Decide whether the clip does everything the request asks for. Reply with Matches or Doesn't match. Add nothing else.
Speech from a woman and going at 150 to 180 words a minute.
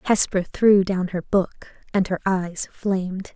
Matches